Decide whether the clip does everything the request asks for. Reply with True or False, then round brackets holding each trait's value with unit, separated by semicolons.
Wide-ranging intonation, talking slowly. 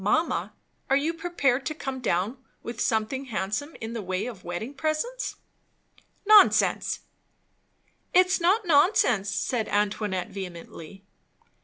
True (7.5 semitones; 120 wpm)